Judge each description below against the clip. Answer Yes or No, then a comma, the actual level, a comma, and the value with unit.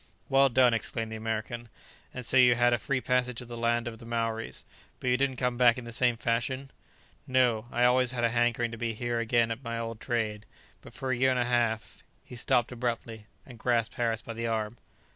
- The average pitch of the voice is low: Yes, low, 120 Hz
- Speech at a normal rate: No, fast, 225 wpm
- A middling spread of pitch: No, narrow, 1.5 semitones